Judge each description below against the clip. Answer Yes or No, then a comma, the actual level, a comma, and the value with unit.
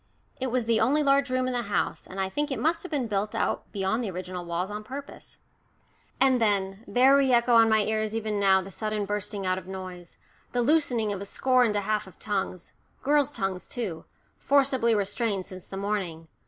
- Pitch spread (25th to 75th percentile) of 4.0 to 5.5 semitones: Yes, average, 4.7 semitones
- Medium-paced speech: No, fast, 210 wpm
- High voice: Yes, high, 215 Hz